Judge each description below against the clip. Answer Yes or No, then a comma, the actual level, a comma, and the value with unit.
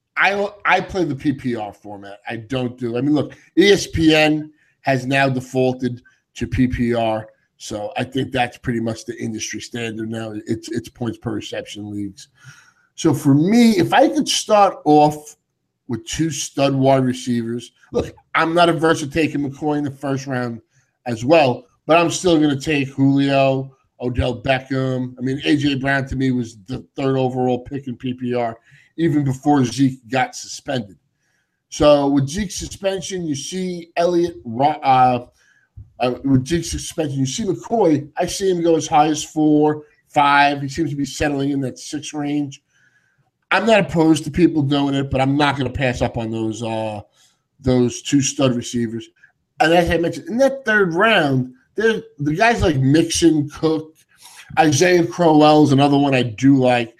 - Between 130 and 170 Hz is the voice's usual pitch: Yes, medium, 140 Hz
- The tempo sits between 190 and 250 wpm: No, average, 170 wpm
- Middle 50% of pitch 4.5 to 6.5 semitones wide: No, average, 3.9 semitones